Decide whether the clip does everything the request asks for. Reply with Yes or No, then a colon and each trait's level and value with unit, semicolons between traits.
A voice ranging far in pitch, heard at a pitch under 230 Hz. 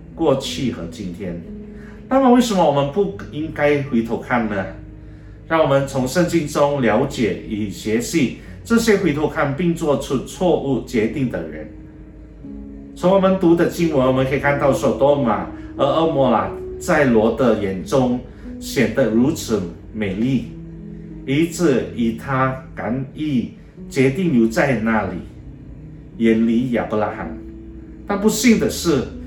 Yes: wide, 7.2 semitones; low, 135 Hz